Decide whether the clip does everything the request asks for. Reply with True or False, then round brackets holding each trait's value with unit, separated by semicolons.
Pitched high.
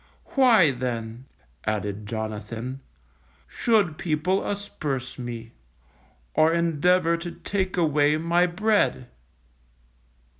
False (155 Hz)